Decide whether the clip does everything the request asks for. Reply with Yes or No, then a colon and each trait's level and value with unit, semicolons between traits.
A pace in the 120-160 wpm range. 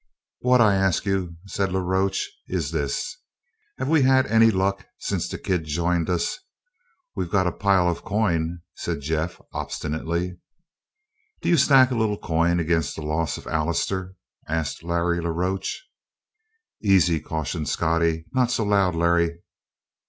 Yes: average, 150 wpm